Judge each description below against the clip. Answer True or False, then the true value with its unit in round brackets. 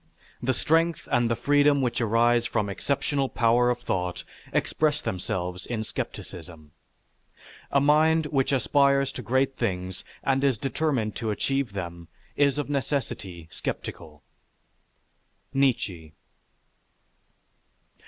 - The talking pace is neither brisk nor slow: False (115 wpm)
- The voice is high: False (120 Hz)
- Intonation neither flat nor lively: False (5.9 semitones)